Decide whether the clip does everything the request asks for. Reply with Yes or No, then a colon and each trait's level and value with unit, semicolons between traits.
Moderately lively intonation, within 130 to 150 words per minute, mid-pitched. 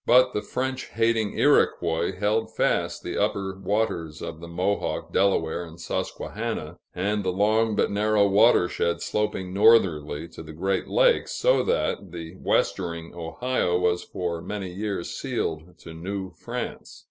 No: average, 3.9 semitones; average, 145 wpm; very low, 95 Hz